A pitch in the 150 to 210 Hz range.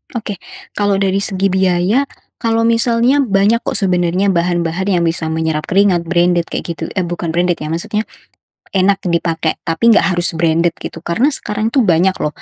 Yes: medium, 185 Hz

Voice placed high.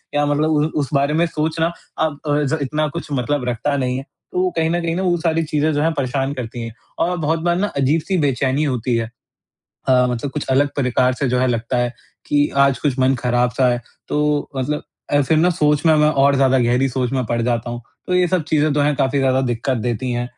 No: medium, 140 Hz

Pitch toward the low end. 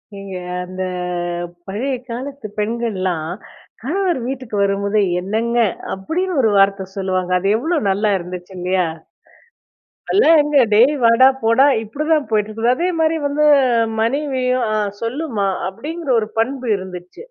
No: high, 230 Hz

